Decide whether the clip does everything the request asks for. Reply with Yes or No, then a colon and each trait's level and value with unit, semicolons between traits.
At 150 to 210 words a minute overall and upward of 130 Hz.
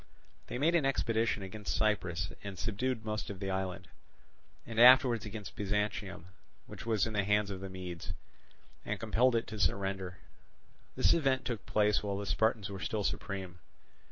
No: average, 165 wpm; low, 105 Hz